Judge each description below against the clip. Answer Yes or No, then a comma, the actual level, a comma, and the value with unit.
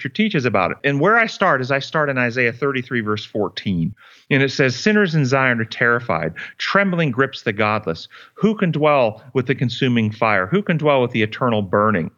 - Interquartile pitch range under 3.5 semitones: No, average, 5.1 semitones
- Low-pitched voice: Yes, low, 130 Hz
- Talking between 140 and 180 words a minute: No, average, 200 wpm